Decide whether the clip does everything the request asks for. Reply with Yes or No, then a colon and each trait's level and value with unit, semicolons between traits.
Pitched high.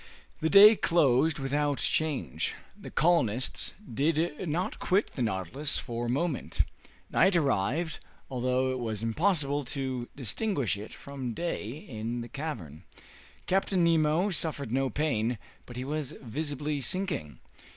No: medium, 140 Hz